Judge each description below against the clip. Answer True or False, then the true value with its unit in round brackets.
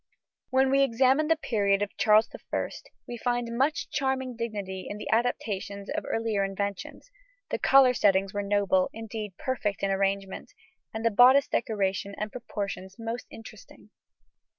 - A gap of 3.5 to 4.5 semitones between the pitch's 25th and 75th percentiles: True (3.9 semitones)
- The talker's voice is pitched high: True (220 Hz)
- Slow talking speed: False (150 wpm)